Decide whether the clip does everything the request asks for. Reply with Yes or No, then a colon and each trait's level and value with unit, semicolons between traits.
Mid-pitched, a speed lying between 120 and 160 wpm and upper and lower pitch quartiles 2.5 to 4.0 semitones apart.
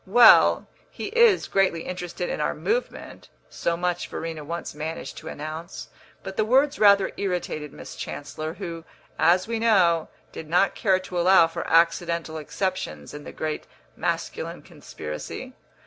Yes: medium, 170 Hz; average, 150 wpm; average, 3.4 semitones